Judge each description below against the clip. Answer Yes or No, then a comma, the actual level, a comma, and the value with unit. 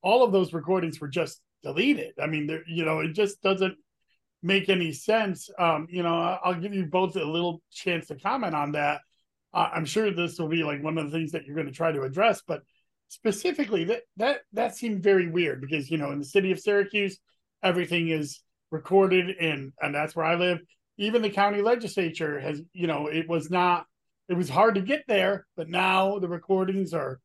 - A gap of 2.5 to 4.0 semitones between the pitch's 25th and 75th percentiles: Yes, average, 3.7 semitones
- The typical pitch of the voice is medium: Yes, medium, 180 Hz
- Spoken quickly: Yes, fast, 215 wpm